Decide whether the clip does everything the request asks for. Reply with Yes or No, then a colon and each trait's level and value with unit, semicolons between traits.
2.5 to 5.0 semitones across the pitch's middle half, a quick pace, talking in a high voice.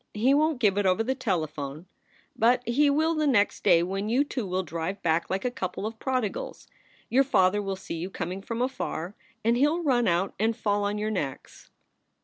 No: wide, 5.4 semitones; fast, 210 wpm; high, 210 Hz